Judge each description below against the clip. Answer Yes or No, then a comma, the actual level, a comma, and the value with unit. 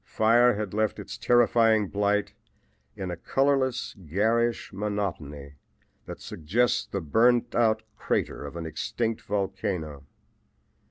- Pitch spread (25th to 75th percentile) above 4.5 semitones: Yes, average, 4.9 semitones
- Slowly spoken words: Yes, slow, 115 wpm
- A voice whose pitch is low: Yes, low, 105 Hz